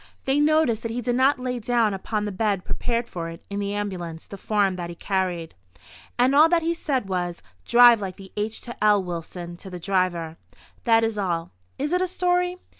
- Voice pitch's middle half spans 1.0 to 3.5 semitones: No, average, 5.3 semitones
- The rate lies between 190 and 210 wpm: Yes, average, 195 wpm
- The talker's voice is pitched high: Yes, high, 210 Hz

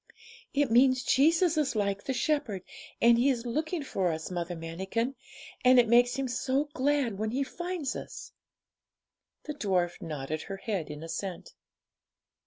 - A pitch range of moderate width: No, wide, 6.4 semitones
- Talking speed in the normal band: Yes, average, 155 wpm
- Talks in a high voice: Yes, high, 240 Hz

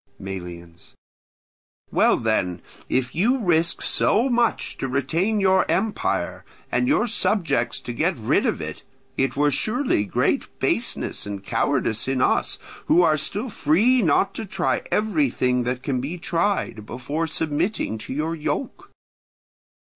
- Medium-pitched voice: Yes, medium, 155 Hz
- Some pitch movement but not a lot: No, wide, 8.3 semitones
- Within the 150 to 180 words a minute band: No, average, 140 wpm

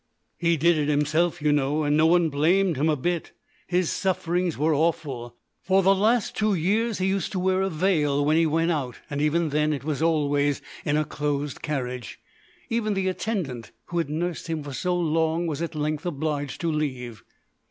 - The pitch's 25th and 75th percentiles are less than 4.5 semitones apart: Yes, average, 3.2 semitones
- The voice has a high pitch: No, medium, 160 Hz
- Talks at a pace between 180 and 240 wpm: Yes, average, 195 wpm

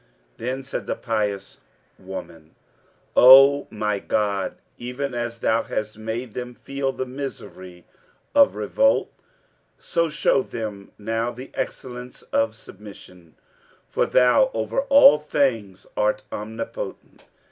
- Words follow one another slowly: Yes, slow, 115 wpm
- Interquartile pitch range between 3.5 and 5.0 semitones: Yes, average, 4.1 semitones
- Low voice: Yes, low, 115 Hz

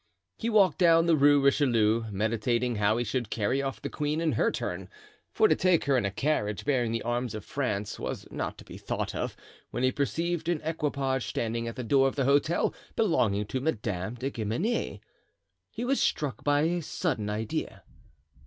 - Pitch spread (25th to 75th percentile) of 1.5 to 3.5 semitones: No, wide, 5.5 semitones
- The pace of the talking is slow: No, average, 190 wpm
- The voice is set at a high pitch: No, low, 130 Hz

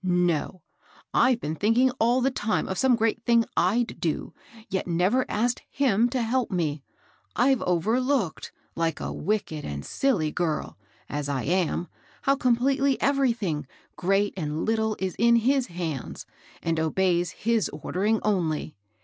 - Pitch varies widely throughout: Yes, wide, 6.2 semitones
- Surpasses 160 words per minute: No, average, 150 wpm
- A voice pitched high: Yes, high, 205 Hz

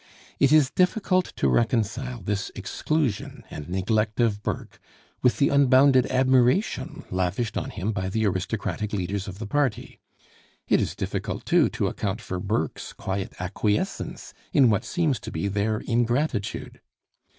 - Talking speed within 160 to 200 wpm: No, average, 145 wpm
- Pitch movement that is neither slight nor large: Yes, average, 4.8 semitones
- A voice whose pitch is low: Yes, low, 110 Hz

